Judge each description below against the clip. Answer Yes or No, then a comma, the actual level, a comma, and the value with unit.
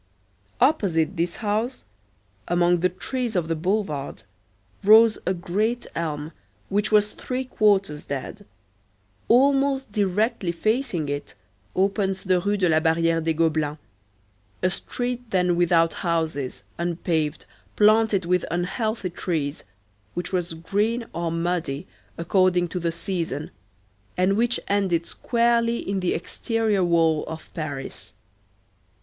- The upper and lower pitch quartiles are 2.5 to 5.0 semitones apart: Yes, average, 4.3 semitones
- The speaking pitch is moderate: Yes, medium, 180 Hz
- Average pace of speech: No, slow, 120 wpm